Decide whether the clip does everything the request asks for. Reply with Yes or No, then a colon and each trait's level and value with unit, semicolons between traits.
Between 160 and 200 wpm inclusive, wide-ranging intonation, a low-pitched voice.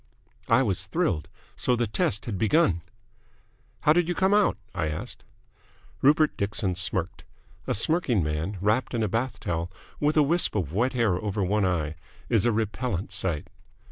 Yes: average, 170 wpm; wide, 6.1 semitones; low, 105 Hz